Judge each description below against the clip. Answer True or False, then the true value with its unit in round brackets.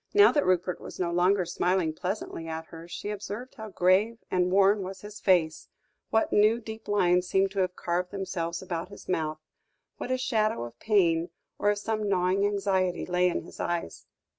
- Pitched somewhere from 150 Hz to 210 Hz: True (185 Hz)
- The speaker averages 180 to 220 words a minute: True (190 wpm)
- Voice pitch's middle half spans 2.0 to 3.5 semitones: True (2.8 semitones)